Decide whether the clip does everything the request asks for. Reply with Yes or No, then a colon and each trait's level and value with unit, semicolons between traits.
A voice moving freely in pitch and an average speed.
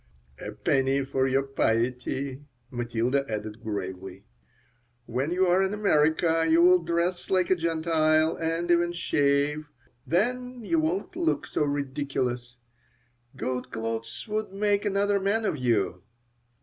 No: wide, 6.4 semitones; slow, 125 wpm